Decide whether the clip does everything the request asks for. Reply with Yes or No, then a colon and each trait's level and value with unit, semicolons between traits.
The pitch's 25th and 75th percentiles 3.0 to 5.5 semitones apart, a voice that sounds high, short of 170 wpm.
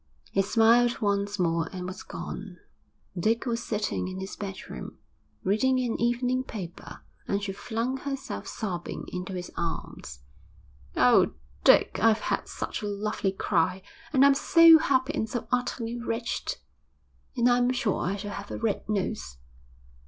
Yes: average, 4.2 semitones; high, 215 Hz; average, 150 wpm